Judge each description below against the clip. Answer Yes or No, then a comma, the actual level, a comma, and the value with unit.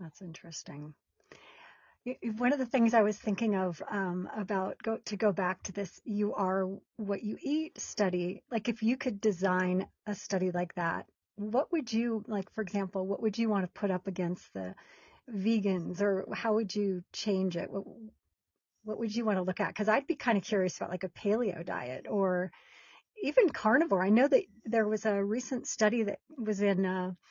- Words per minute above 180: Yes, average, 200 wpm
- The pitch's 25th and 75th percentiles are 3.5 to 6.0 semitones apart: No, average, 3.0 semitones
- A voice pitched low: No, high, 205 Hz